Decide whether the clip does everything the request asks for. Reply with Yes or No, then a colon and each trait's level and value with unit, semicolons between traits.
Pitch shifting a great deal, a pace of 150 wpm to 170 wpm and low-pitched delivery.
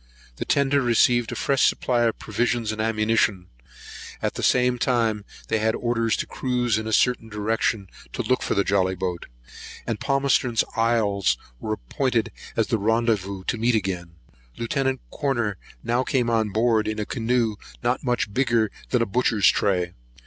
No: average, 2.7 semitones; average, 165 wpm; low, 115 Hz